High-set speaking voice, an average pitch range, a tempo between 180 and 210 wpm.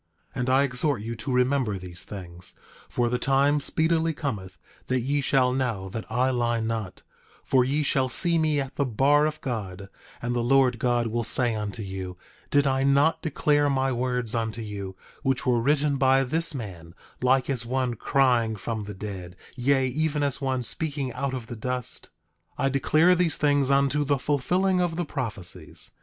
No: low, 130 Hz; average, 3.7 semitones; average, 185 wpm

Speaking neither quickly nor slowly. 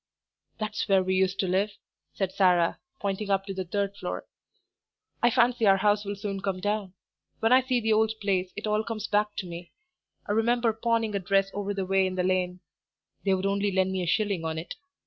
No: fast, 215 wpm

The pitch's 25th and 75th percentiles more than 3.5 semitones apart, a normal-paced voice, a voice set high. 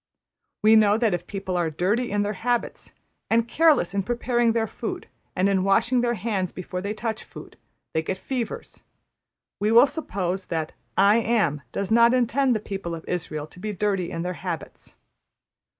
Yes: average, 4.3 semitones; average, 180 wpm; high, 205 Hz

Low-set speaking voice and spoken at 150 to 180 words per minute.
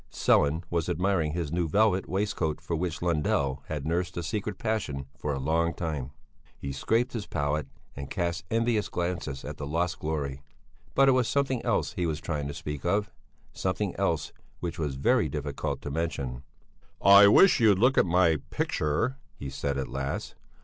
Yes: very low, 85 Hz; average, 175 wpm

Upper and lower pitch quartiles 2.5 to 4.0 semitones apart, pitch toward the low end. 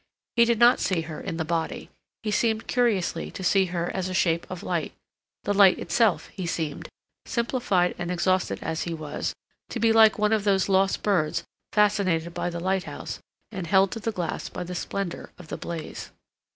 No: average, 3.5 semitones; medium, 185 Hz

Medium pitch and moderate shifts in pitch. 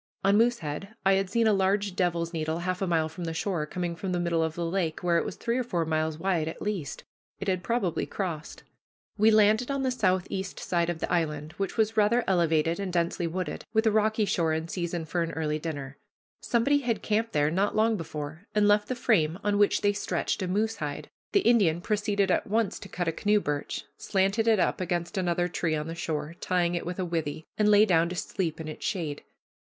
Yes: medium, 180 Hz; average, 4.1 semitones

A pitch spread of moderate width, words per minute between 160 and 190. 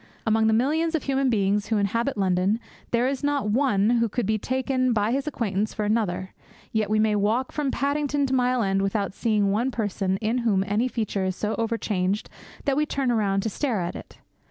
No: average, 4.2 semitones; fast, 205 wpm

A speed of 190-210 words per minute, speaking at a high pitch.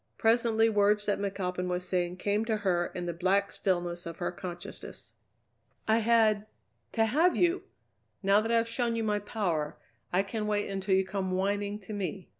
No: average, 180 wpm; high, 200 Hz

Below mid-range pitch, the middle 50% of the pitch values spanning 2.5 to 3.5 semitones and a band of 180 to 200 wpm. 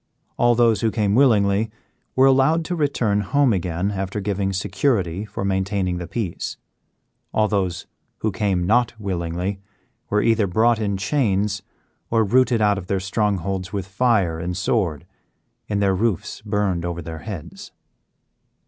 No: low, 100 Hz; average, 3.2 semitones; average, 150 wpm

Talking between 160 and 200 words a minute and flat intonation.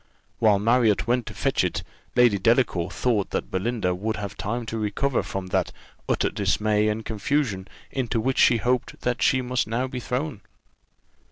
No: average, 170 wpm; average, 3.2 semitones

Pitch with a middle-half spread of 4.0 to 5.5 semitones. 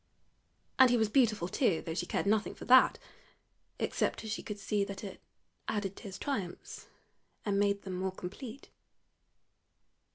No: average, 2.8 semitones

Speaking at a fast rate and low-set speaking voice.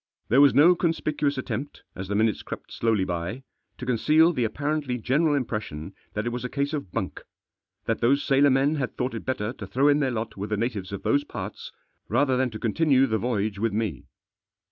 Yes: fast, 210 wpm; low, 125 Hz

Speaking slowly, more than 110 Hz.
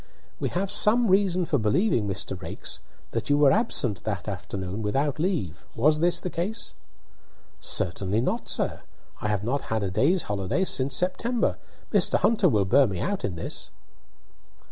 No: average, 165 wpm; low, 135 Hz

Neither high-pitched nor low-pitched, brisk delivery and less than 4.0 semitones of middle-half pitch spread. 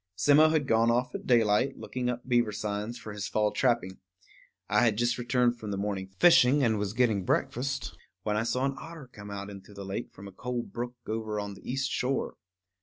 No: low, 115 Hz; fast, 210 wpm; average, 3.4 semitones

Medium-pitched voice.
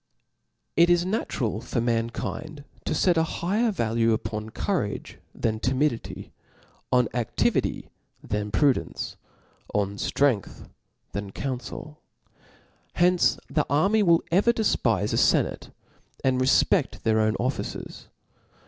No: low, 130 Hz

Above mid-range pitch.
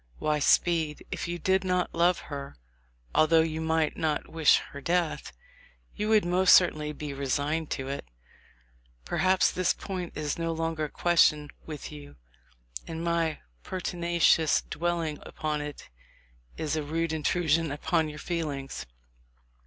No: medium, 160 Hz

